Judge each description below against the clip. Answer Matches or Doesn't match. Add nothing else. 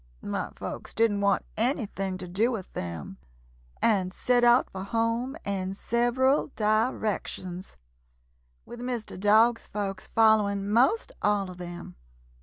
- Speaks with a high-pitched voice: Matches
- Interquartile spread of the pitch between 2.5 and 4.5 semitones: Matches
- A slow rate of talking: Matches